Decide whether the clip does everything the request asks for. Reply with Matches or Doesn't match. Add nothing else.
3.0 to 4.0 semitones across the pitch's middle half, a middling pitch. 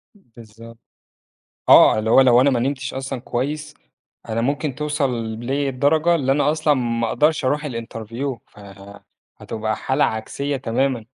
Doesn't match